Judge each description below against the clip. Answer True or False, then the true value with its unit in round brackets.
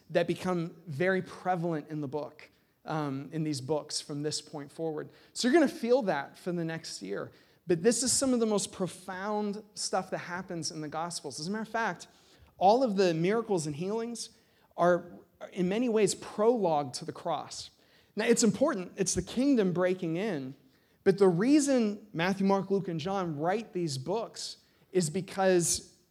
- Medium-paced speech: True (180 wpm)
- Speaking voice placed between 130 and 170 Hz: False (185 Hz)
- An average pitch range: True (4.6 semitones)